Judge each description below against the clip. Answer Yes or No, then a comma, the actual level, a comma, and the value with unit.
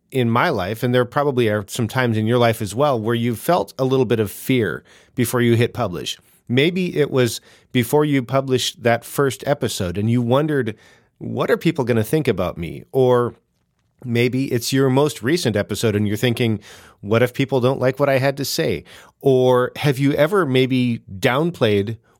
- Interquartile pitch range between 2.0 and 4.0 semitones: Yes, average, 2.9 semitones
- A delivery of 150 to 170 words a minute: No, average, 195 wpm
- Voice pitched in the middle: No, low, 125 Hz